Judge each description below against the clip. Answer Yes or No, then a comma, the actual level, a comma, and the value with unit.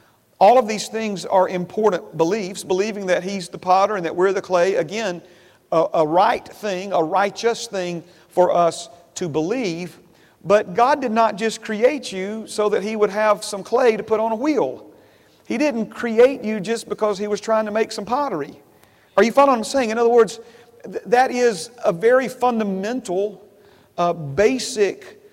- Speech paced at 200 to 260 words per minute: No, average, 185 wpm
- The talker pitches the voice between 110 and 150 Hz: No, high, 210 Hz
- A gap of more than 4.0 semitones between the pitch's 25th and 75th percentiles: No, average, 3.6 semitones